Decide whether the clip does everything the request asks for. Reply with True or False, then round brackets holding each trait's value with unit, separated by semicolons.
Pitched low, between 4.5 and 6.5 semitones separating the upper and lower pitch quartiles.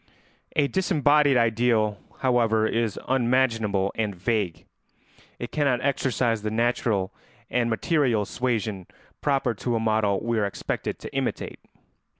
False (115 Hz; 3.1 semitones)